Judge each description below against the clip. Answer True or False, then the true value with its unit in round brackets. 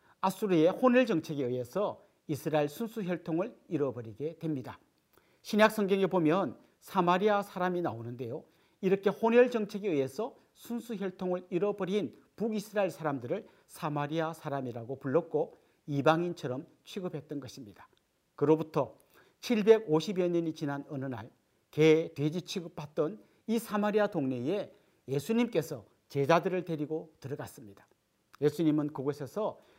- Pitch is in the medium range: True (165 Hz)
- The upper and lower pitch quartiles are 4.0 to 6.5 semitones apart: True (5.5 semitones)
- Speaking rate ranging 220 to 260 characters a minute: False (310 characters per minute)